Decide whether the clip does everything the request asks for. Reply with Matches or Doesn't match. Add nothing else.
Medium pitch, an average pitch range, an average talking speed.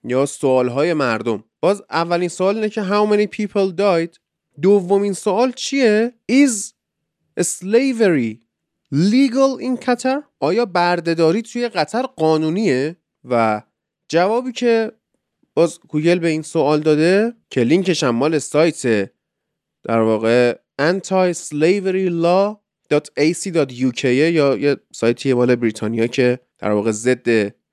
Doesn't match